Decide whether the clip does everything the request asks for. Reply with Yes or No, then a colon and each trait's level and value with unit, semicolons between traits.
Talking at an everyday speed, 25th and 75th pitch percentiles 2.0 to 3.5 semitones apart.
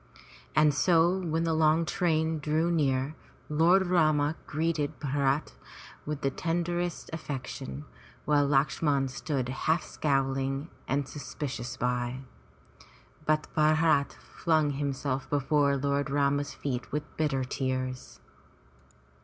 No: slow, 110 wpm; average, 2.8 semitones